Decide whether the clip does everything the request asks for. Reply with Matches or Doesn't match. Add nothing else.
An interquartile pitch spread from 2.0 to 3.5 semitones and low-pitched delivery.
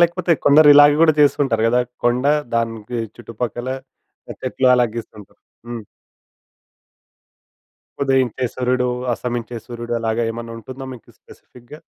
Matches